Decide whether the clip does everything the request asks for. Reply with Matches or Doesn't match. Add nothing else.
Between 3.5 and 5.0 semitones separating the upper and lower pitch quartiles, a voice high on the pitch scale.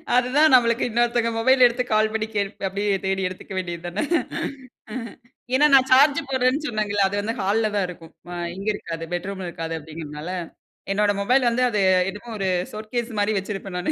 Matches